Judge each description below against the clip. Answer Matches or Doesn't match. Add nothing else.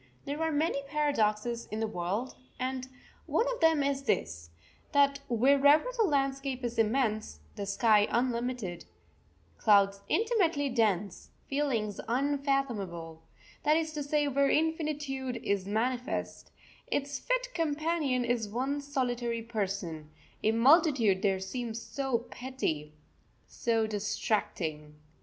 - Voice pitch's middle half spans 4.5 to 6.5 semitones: Matches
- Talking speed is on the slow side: Matches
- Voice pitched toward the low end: Doesn't match